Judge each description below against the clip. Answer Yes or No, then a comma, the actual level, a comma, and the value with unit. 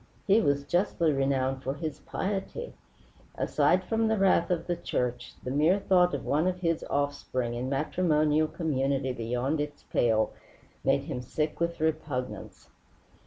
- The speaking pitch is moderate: Yes, medium, 150 Hz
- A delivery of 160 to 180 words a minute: No, average, 150 wpm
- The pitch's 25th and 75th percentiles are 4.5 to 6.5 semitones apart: Yes, average, 4.8 semitones